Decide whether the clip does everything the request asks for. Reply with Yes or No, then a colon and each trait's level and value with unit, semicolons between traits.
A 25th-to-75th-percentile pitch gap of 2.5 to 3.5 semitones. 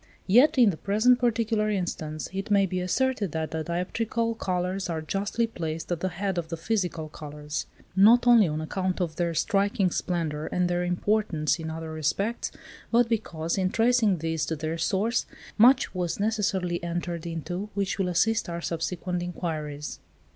No: average, 4.4 semitones